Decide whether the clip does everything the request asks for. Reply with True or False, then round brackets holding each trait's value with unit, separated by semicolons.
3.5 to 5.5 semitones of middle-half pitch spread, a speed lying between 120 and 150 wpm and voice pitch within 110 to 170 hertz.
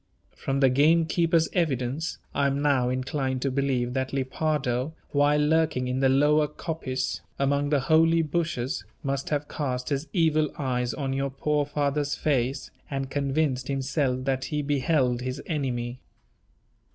False (2.5 semitones; 145 wpm; 140 Hz)